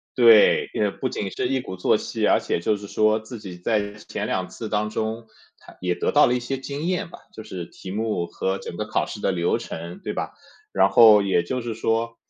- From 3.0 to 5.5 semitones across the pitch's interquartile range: Yes, average, 3.9 semitones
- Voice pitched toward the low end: Yes, low, 110 Hz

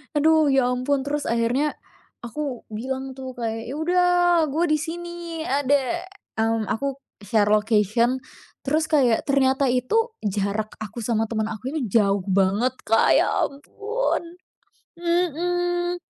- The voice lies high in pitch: Yes, very high, 265 Hz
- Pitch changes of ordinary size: No, wide, 6.1 semitones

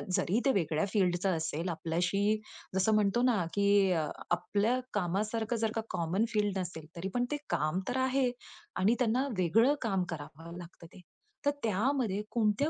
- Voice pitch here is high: Yes, high, 200 Hz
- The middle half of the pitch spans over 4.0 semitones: Yes, average, 4.5 semitones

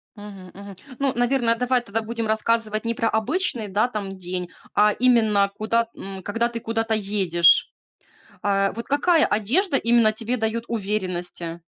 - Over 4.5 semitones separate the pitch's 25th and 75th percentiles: No, average, 2.8 semitones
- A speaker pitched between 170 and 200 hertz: No, high, 220 Hz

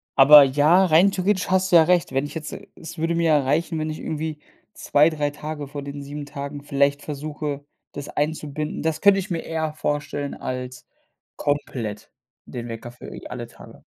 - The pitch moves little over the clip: Yes, narrow, 2.2 semitones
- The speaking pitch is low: No, medium, 150 Hz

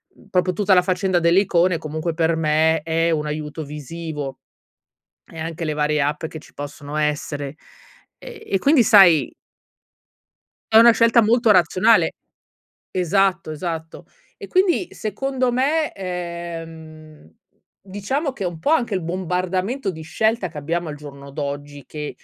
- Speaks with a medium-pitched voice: Yes, medium, 170 Hz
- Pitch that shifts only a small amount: No, average, 4.3 semitones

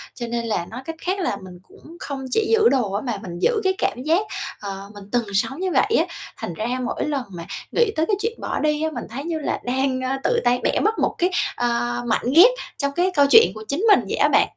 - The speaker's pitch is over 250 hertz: Yes, very high, 270 Hz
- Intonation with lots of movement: Yes, wide, 7.0 semitones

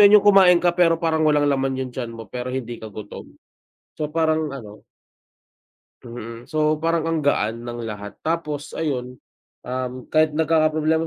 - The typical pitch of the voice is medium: Yes, medium, 150 Hz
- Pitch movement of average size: Yes, average, 4.7 semitones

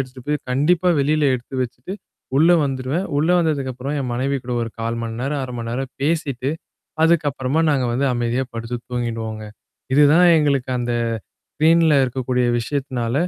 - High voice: No, low, 130 Hz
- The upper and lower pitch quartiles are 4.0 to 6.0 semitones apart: No, average, 3.4 semitones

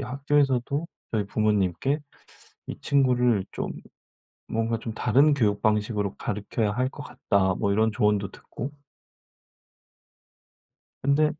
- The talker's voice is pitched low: Yes, low, 115 Hz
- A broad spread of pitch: No, average, 4.7 semitones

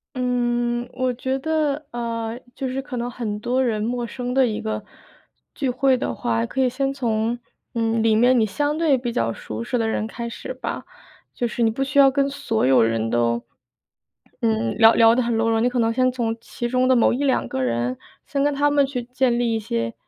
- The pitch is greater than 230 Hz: Yes, high, 240 Hz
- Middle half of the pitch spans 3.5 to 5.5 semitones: No, narrow, 2.6 semitones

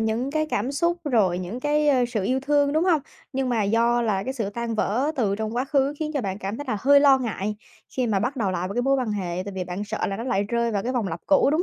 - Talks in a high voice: Yes, high, 235 Hz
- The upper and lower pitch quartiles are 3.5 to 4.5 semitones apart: No, average, 5.2 semitones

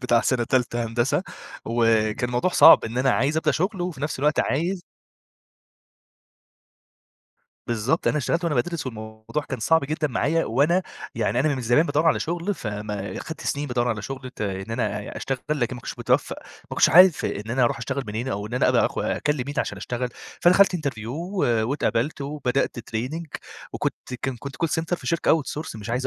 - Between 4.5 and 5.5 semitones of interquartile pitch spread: Yes, average, 5.1 semitones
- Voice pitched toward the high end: No, low, 130 Hz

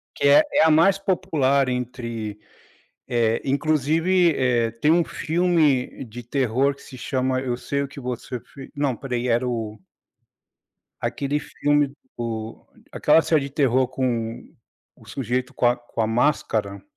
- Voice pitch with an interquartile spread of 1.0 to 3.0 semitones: No, average, 3.4 semitones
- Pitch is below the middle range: Yes, low, 130 Hz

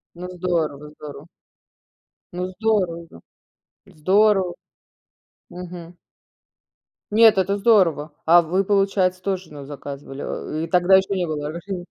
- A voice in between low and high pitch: Yes, medium, 180 Hz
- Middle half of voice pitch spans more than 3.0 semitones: Yes, average, 3.5 semitones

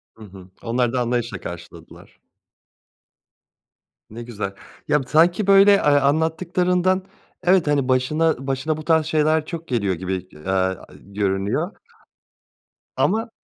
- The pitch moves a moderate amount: No, wide, 8.1 semitones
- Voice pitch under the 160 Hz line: Yes, low, 135 Hz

